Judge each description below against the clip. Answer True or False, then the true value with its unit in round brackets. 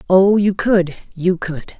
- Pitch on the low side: False (185 Hz)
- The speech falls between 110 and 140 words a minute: True (135 wpm)